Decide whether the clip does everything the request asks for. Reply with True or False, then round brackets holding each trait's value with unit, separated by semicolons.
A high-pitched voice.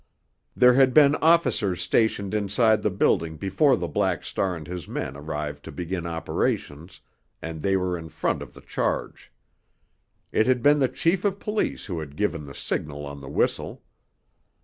False (95 Hz)